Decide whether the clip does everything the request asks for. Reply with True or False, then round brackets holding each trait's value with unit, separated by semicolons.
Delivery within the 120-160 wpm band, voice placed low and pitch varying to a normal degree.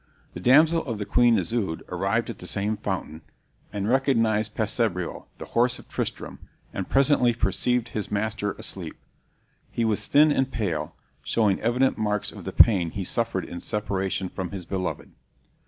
True (155 wpm; 110 Hz; 3.9 semitones)